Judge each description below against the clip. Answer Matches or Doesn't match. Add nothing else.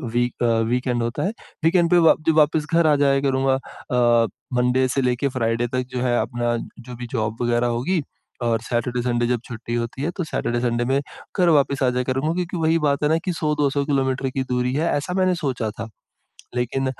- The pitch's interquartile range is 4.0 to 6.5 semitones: Doesn't match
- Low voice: Matches